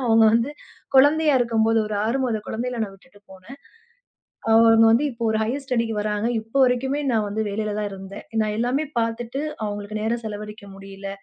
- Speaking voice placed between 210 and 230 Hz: Yes, high, 225 Hz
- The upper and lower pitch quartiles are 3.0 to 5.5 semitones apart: No, narrow, 2.6 semitones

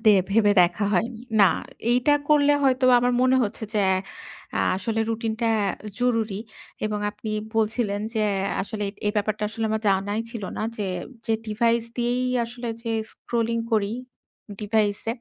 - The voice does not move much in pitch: Yes, narrow, 2.3 semitones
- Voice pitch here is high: Yes, high, 225 Hz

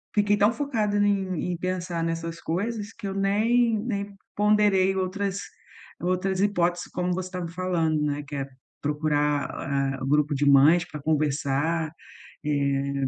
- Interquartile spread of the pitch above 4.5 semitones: Yes, average, 5.1 semitones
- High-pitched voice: No, medium, 180 Hz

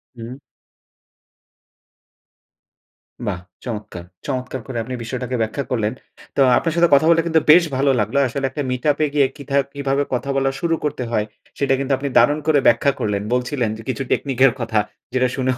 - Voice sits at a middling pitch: No, low, 130 Hz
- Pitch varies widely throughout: No, average, 2.9 semitones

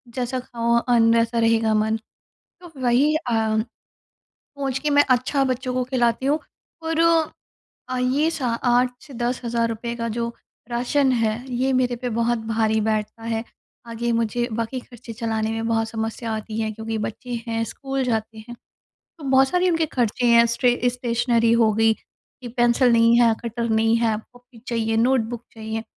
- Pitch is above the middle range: Yes, high, 235 Hz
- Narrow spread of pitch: Yes, narrow, 2.0 semitones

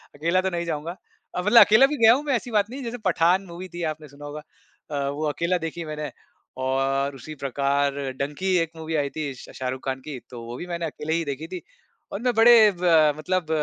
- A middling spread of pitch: Yes, average, 4.4 semitones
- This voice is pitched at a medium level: Yes, medium, 160 Hz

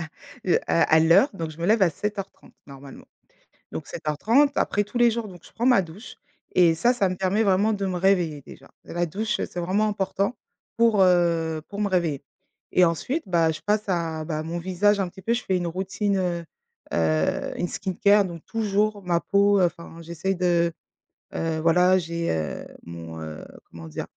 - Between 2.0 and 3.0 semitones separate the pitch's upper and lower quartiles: No, average, 3.7 semitones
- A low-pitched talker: No, medium, 180 Hz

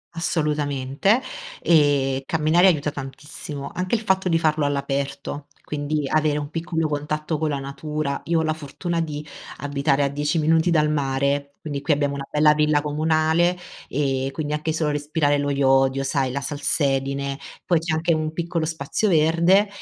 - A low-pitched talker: No, medium, 150 Hz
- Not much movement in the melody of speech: Yes, narrow, 2.3 semitones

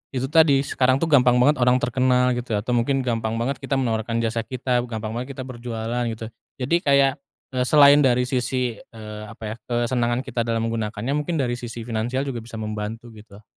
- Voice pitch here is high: No, low, 120 Hz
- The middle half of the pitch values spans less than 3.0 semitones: Yes, narrow, 2.4 semitones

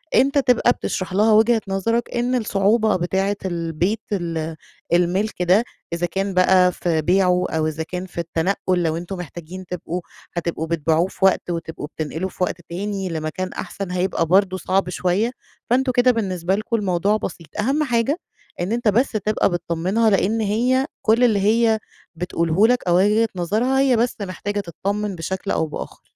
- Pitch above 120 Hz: Yes, high, 190 Hz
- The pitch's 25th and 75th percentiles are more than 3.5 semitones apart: Yes, average, 4.0 semitones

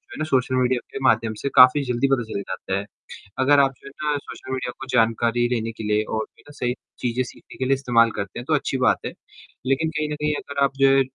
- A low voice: Yes, low, 130 Hz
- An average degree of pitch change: Yes, average, 3.0 semitones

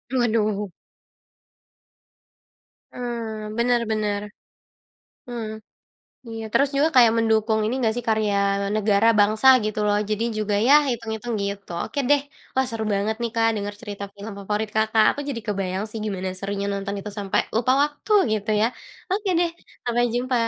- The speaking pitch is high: Yes, high, 220 Hz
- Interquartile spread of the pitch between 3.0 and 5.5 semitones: No, narrow, 2.4 semitones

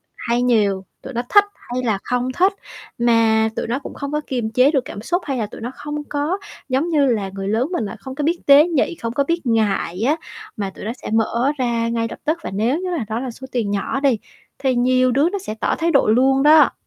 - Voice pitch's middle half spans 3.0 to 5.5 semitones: Yes, average, 4.4 semitones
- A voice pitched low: No, very high, 255 Hz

